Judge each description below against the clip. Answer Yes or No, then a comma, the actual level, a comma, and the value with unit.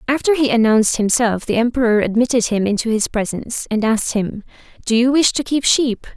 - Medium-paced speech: Yes, average, 195 wpm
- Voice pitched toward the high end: Yes, high, 235 Hz